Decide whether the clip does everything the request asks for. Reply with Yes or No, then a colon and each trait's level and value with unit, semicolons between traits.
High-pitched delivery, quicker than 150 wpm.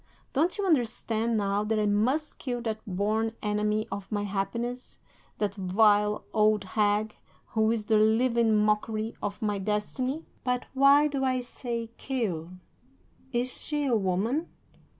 No: high, 220 Hz; average, 145 wpm